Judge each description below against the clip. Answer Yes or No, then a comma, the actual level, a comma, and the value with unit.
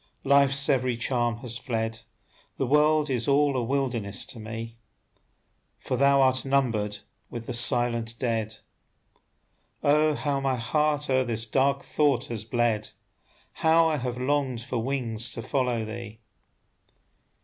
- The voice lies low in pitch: Yes, low, 125 Hz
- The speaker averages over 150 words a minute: No, average, 140 wpm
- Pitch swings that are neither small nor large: Yes, average, 3.2 semitones